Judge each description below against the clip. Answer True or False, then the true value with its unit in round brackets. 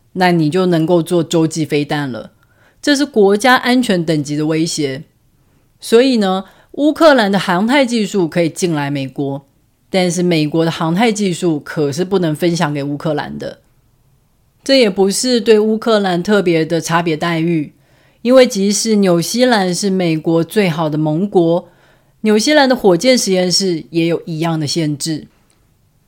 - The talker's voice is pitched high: False (170 Hz)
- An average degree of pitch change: True (5.0 semitones)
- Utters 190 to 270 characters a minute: True (240 characters per minute)